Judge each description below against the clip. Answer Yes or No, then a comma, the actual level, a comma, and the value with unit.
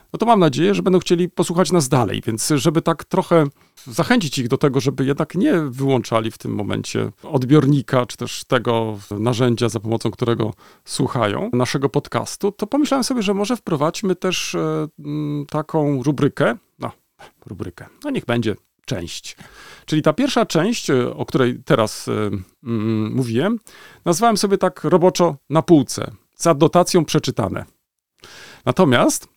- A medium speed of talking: Yes, average, 145 wpm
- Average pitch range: No, wide, 6.3 semitones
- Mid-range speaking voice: Yes, medium, 150 Hz